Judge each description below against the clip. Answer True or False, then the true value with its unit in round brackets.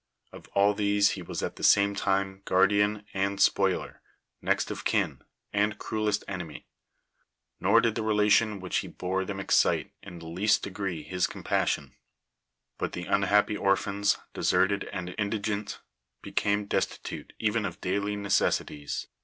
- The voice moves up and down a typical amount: False (1.4 semitones)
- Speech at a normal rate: True (145 wpm)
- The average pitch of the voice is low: True (100 Hz)